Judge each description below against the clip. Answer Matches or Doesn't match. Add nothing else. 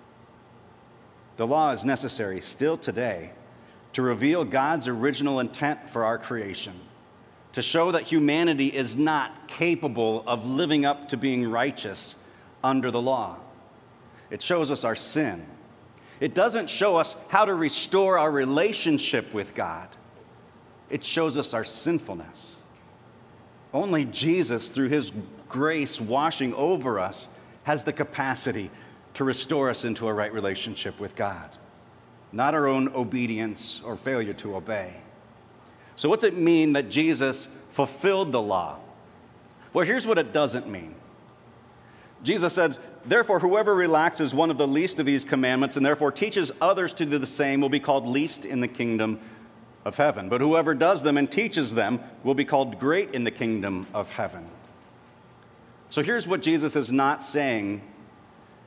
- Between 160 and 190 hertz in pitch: Doesn't match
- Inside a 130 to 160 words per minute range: Matches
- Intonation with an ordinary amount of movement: Matches